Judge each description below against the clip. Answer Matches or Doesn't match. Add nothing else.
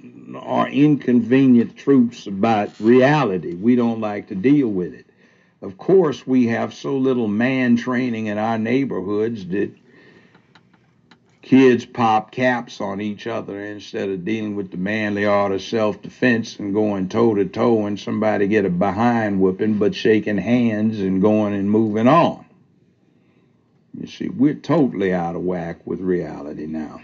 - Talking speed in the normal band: Matches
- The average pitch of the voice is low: Matches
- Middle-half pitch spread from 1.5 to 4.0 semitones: Matches